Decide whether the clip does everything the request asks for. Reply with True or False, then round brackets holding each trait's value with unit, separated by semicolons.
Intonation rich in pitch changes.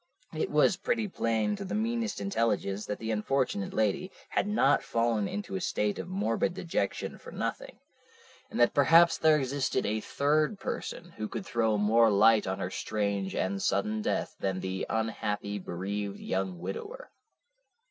True (8.0 semitones)